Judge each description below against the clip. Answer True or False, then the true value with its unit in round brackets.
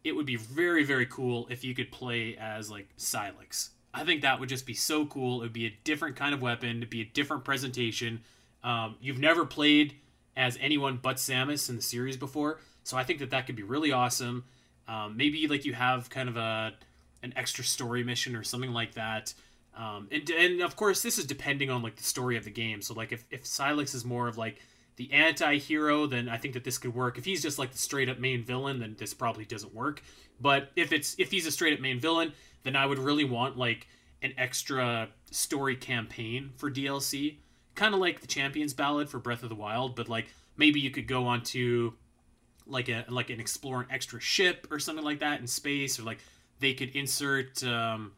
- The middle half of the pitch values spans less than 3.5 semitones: True (3.1 semitones)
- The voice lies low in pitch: True (130 Hz)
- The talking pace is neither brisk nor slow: False (225 wpm)